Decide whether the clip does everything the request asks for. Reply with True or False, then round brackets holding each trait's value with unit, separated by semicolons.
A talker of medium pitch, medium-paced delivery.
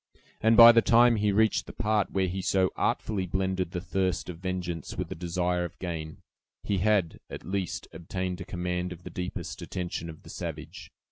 False (90 Hz; 195 wpm)